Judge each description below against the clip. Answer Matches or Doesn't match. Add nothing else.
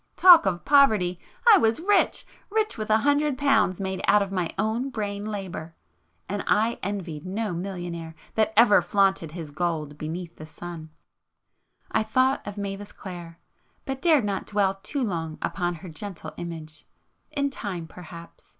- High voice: Matches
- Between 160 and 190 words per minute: Doesn't match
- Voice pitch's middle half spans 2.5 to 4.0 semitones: Doesn't match